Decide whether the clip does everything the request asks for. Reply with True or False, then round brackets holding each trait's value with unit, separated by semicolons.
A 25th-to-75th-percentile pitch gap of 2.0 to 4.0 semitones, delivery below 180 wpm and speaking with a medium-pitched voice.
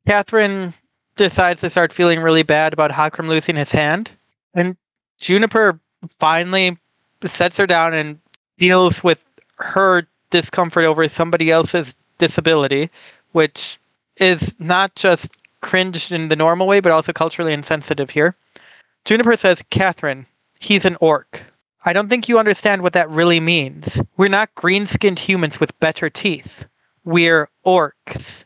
True (2.8 semitones; 135 wpm; 170 Hz)